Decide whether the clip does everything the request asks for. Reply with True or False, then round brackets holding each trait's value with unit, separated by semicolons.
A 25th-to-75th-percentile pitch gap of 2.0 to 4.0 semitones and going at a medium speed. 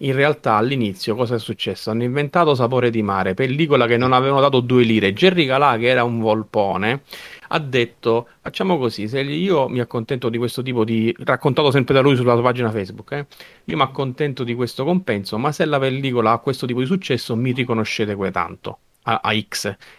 False (3.5 semitones; 200 wpm)